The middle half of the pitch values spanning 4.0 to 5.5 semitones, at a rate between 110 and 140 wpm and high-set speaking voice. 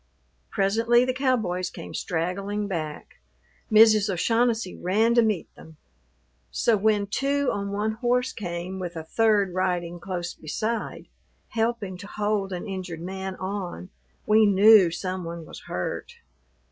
No: average, 3.6 semitones; slow, 135 wpm; high, 200 Hz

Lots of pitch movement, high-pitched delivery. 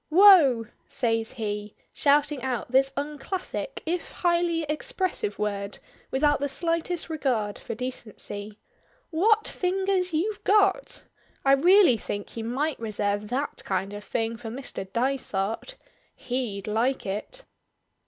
Yes: wide, 7.6 semitones; very high, 265 Hz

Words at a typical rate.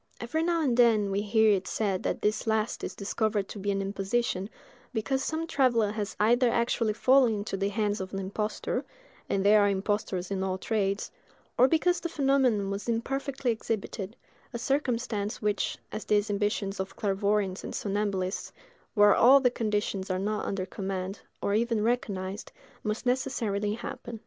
Yes: average, 165 wpm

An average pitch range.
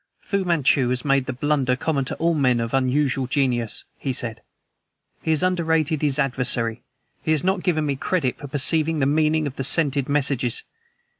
Yes: average, 3.5 semitones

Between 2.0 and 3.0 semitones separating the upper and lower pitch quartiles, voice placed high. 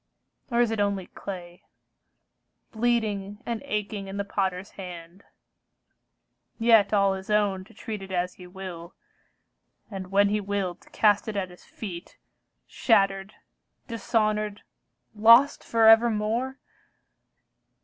Yes: narrow, 2.4 semitones; high, 205 Hz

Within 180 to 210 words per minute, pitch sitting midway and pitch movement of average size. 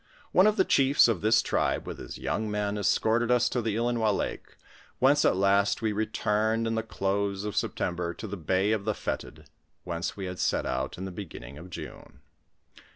No: average, 200 wpm; low, 105 Hz; average, 3.0 semitones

